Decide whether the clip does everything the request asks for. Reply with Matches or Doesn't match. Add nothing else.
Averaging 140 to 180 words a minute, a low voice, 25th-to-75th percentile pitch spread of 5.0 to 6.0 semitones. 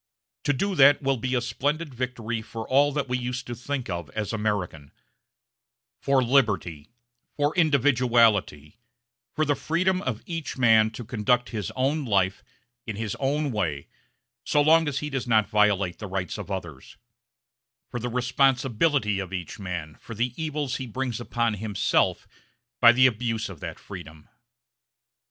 Doesn't match